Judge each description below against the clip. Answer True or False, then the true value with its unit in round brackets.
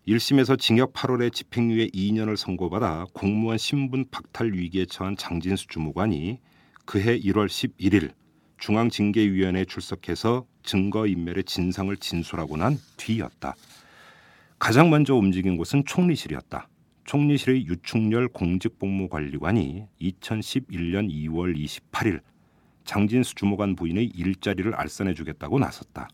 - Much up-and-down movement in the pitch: False (4.5 semitones)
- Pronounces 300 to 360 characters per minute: False (285 characters per minute)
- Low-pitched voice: True (100 Hz)